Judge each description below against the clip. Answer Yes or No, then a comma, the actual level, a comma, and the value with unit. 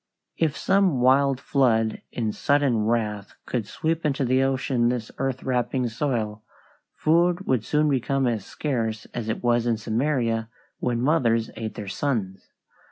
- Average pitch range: Yes, average, 3.7 semitones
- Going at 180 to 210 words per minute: No, average, 150 wpm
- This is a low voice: Yes, low, 125 Hz